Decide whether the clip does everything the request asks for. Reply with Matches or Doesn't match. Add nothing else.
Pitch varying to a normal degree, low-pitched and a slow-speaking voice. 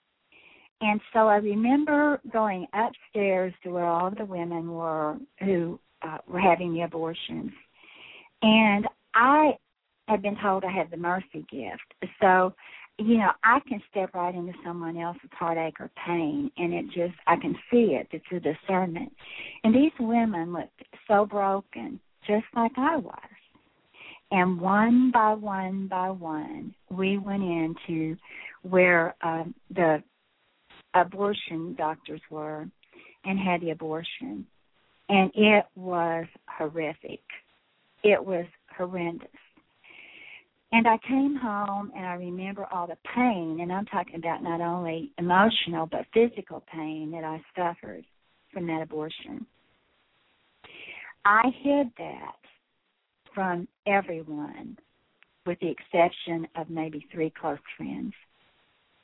Doesn't match